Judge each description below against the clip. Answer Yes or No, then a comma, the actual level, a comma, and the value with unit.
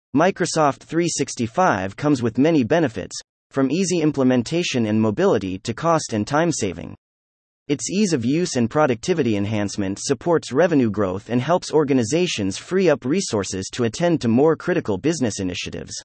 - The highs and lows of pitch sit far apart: Yes, wide, 7.4 semitones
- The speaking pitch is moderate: No, low, 130 Hz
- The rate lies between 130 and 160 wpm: Yes, average, 145 wpm